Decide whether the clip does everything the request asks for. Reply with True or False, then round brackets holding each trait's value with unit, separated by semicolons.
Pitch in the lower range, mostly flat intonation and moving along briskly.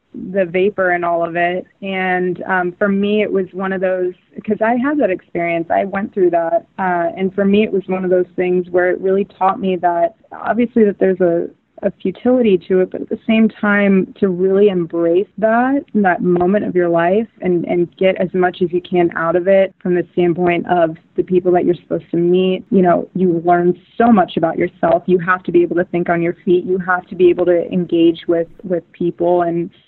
False (185 Hz; 2.1 semitones; 225 wpm)